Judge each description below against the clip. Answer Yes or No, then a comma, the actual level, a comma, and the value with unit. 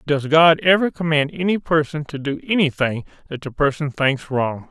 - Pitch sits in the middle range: Yes, medium, 150 Hz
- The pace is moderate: Yes, average, 180 wpm